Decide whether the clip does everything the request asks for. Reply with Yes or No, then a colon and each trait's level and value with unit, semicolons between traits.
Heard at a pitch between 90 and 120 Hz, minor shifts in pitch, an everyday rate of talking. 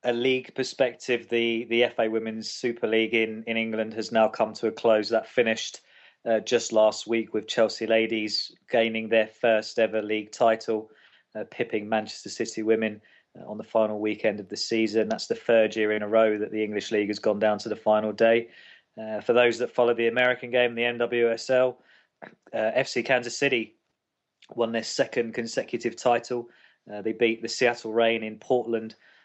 Yes: low, 115 Hz; narrow, 1.3 semitones; average, 185 wpm